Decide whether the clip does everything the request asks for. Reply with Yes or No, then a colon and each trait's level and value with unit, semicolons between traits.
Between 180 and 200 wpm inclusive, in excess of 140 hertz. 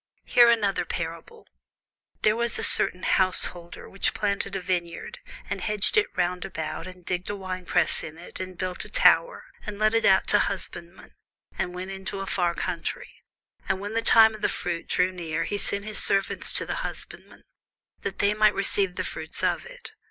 Yes: average, 190 wpm; high, 190 Hz